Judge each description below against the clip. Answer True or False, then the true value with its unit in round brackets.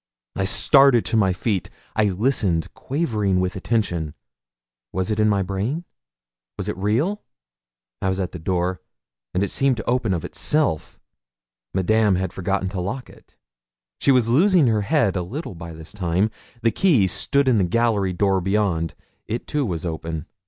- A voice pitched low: True (100 Hz)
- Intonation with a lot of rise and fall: False (4.6 semitones)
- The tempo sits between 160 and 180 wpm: True (170 wpm)